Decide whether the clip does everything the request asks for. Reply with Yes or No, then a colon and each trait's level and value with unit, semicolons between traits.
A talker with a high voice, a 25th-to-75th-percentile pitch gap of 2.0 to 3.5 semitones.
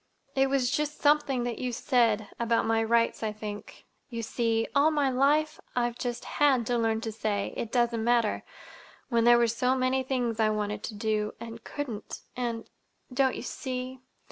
Yes: high, 240 Hz; narrow, 2.6 semitones